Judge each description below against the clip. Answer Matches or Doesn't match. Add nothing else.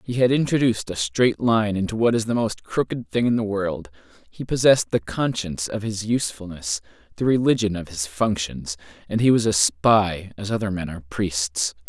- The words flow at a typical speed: Matches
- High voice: Doesn't match